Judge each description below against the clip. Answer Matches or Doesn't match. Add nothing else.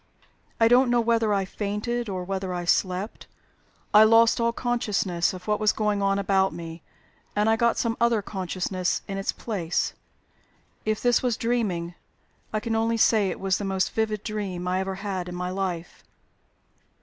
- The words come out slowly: Doesn't match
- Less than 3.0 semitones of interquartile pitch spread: Doesn't match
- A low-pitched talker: Doesn't match